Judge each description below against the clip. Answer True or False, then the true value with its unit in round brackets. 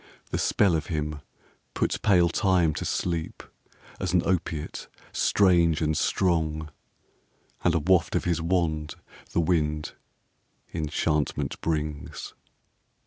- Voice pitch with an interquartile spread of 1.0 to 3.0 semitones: True (2.4 semitones)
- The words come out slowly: True (115 wpm)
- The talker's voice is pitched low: True (80 Hz)